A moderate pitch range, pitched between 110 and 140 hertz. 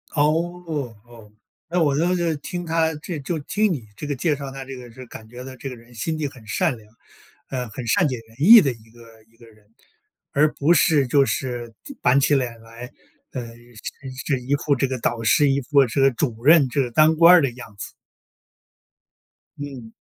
Yes: average, 4.3 semitones; low, 135 Hz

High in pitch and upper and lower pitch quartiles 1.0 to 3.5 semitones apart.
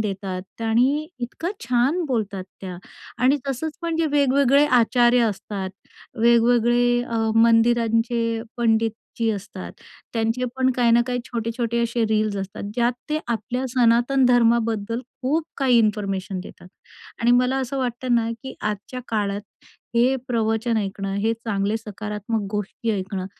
Yes: high, 230 Hz; narrow, 2.5 semitones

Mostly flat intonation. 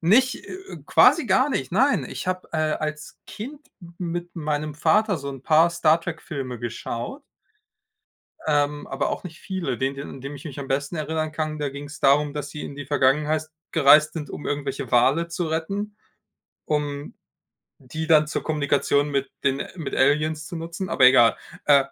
No: average, 3.1 semitones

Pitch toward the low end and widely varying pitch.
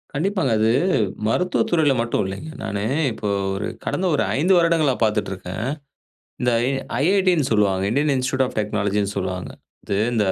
Yes: low, 120 Hz; wide, 7.5 semitones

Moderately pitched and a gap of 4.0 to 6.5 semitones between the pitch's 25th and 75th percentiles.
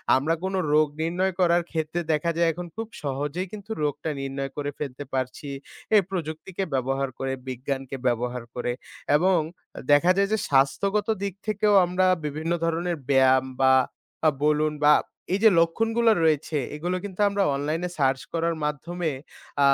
Yes: medium, 155 Hz; average, 4.6 semitones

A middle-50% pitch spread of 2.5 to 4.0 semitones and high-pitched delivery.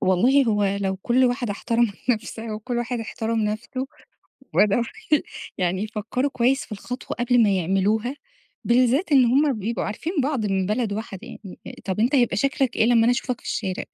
Yes: average, 3.3 semitones; high, 230 Hz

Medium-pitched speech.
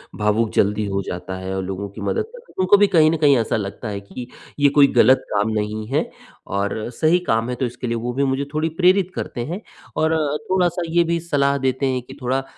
No: low, 130 Hz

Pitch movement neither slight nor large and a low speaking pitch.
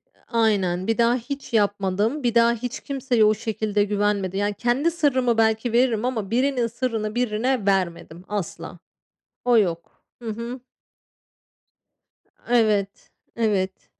No: average, 3.1 semitones; high, 220 Hz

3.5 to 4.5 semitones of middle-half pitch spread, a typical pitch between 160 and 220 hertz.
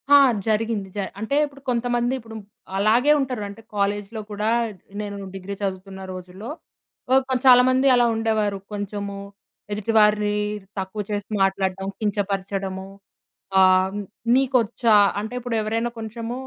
No: average, 2.8 semitones; high, 210 Hz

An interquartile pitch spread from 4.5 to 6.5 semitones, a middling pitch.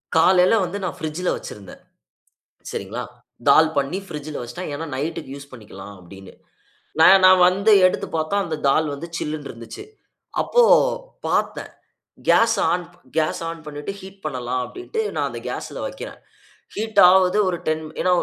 Yes: average, 5.1 semitones; medium, 160 Hz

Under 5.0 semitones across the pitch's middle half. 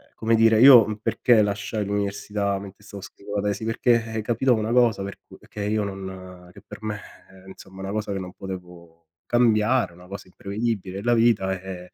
Yes: average, 2.7 semitones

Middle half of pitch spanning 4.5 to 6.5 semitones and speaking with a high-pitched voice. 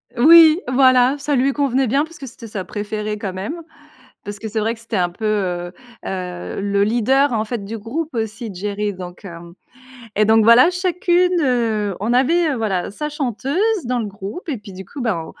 Yes: wide, 5.4 semitones; high, 225 Hz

